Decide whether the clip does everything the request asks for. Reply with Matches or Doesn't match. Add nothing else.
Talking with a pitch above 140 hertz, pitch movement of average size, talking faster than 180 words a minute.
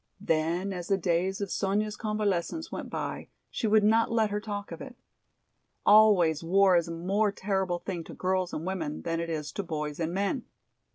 Matches